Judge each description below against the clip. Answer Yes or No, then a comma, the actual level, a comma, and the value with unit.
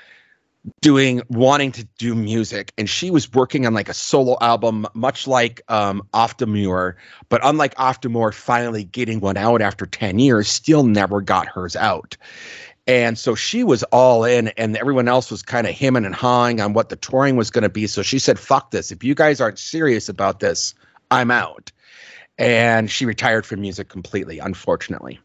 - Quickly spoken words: No, average, 180 wpm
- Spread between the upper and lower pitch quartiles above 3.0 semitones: Yes, average, 3.7 semitones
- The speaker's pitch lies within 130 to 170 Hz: No, low, 115 Hz